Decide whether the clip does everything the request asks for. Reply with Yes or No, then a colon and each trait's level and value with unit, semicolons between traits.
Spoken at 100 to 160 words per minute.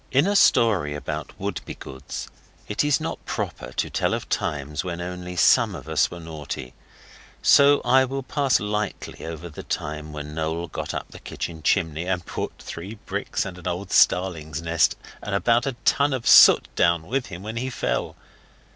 No: average, 180 wpm